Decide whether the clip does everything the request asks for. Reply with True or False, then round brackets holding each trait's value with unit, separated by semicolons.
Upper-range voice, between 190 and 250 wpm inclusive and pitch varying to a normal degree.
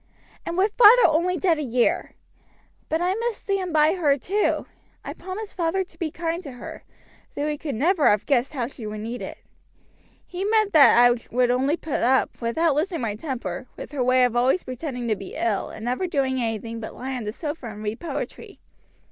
False (280 Hz; 205 wpm; 6.2 semitones)